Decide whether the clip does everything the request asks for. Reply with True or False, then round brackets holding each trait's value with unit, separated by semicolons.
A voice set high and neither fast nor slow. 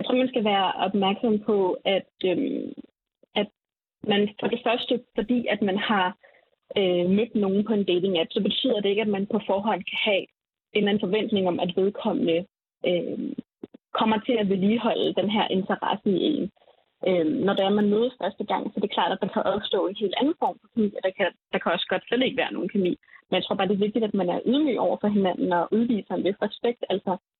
False (210 Hz; 230 wpm)